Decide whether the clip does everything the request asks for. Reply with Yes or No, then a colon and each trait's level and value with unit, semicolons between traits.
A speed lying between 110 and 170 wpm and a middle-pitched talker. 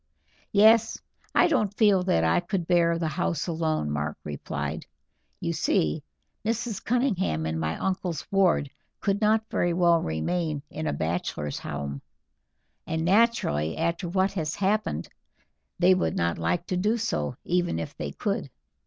Yes: average, 150 wpm; medium, 175 Hz